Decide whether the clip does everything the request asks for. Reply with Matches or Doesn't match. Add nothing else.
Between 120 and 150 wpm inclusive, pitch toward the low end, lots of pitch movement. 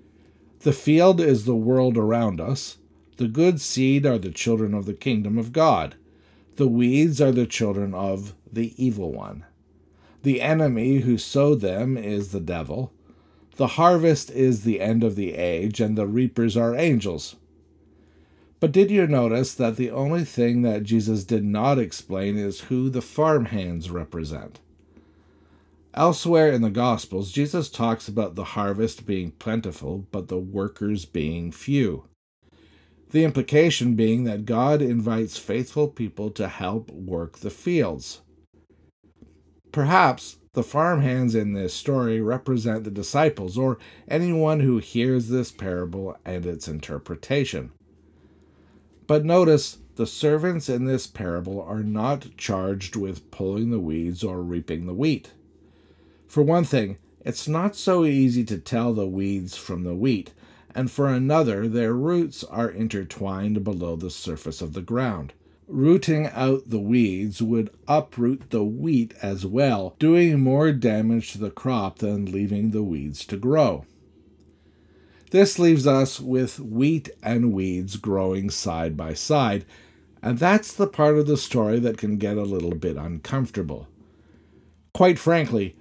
Matches